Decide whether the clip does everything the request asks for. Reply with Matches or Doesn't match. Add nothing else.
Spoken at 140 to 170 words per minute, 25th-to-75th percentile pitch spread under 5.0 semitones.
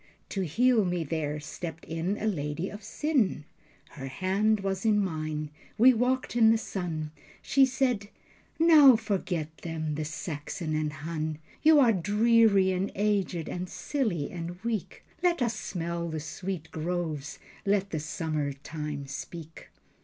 Doesn't match